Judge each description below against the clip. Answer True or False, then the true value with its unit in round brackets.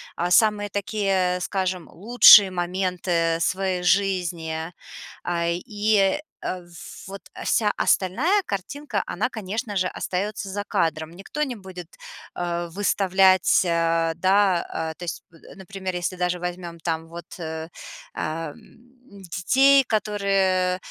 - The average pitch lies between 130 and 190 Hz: True (185 Hz)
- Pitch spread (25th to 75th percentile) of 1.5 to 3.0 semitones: True (2.7 semitones)